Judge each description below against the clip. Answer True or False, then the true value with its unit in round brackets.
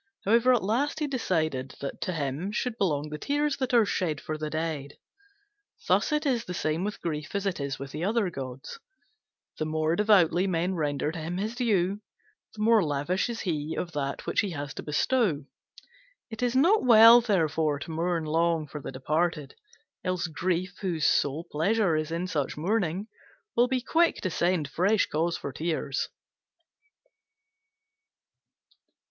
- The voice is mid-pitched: True (175 Hz)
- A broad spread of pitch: True (5.8 semitones)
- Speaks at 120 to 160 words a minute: False (170 wpm)